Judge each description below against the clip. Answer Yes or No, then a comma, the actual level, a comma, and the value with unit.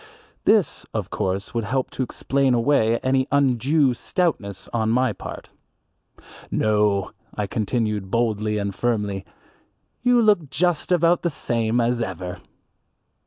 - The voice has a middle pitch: No, low, 120 Hz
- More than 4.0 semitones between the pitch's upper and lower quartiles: Yes, average, 4.9 semitones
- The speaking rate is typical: No, slow, 125 wpm